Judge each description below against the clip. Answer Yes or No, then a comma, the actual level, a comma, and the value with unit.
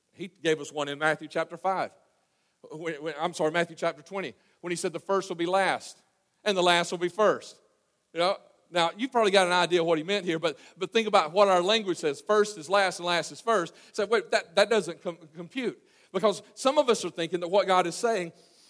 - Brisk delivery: Yes, fast, 235 wpm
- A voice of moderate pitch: Yes, medium, 180 Hz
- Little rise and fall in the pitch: No, average, 3.4 semitones